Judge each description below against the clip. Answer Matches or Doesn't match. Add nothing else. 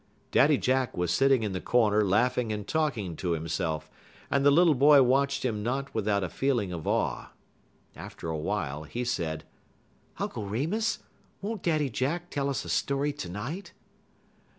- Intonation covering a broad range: Matches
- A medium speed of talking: Matches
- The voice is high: Doesn't match